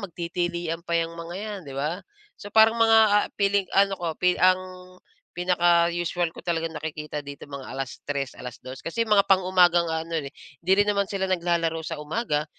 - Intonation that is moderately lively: Yes, average, 3.0 semitones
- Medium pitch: Yes, medium, 170 Hz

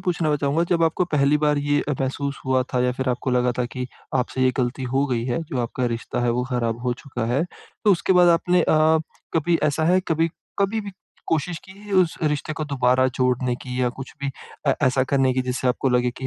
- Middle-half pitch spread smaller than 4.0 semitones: No, average, 4.3 semitones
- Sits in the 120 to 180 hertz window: Yes, low, 135 Hz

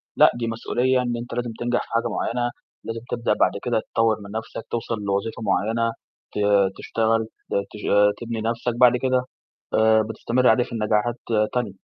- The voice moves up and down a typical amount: No, narrow, 1.5 semitones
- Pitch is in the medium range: No, low, 115 Hz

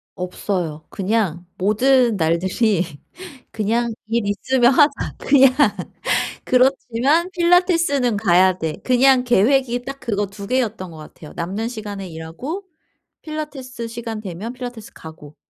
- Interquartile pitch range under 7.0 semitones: Yes, wide, 5.6 semitones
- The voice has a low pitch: No, high, 230 Hz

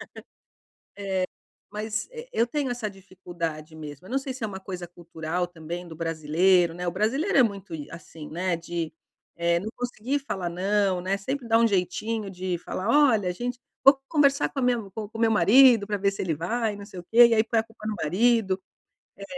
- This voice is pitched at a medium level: No, high, 200 Hz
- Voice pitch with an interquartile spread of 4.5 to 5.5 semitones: Yes, average, 4.9 semitones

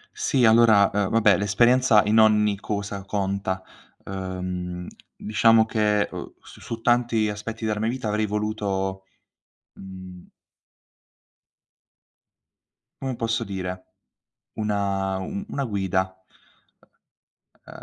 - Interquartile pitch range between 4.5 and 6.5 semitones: No, average, 2.7 semitones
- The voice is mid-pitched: No, low, 105 Hz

